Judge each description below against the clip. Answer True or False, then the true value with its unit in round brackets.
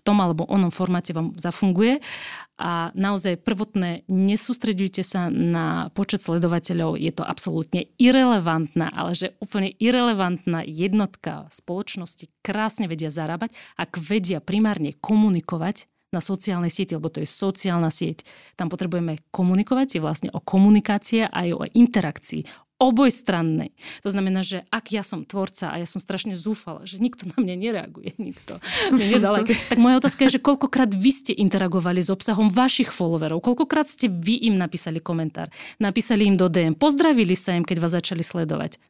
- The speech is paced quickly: False (155 wpm)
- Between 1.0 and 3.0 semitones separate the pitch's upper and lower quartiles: False (4.2 semitones)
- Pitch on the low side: False (195 Hz)